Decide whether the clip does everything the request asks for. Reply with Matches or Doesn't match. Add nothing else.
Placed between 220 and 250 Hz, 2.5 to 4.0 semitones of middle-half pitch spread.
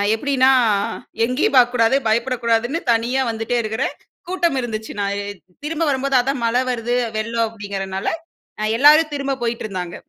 Matches